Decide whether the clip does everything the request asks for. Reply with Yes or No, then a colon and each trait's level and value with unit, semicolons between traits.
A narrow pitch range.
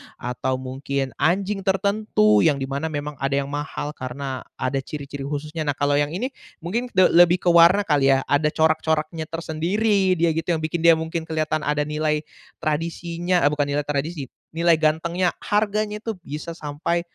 No: average, 3.2 semitones